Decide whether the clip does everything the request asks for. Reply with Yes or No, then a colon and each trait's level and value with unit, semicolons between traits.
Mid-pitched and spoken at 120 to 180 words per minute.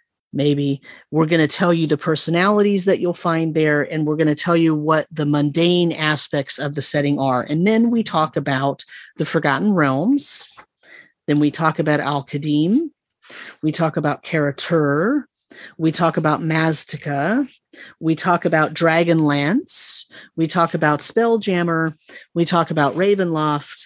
Yes: medium, 160 Hz; average, 155 wpm